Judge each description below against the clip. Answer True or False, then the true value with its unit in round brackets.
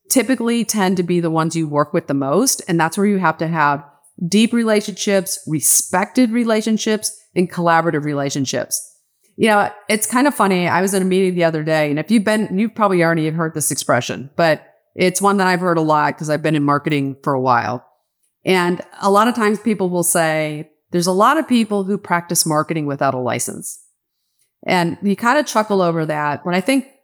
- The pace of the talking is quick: True (210 wpm)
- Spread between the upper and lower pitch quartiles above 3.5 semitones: True (5.2 semitones)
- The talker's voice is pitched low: False (180 Hz)